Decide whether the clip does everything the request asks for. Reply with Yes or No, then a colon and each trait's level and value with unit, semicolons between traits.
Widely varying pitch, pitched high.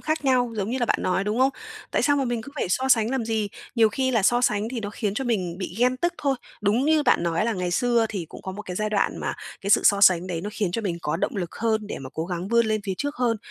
No: average, 4.3 semitones; high, 220 Hz